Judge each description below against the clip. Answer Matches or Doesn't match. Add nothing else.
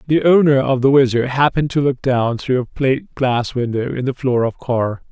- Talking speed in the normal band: Doesn't match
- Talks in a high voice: Doesn't match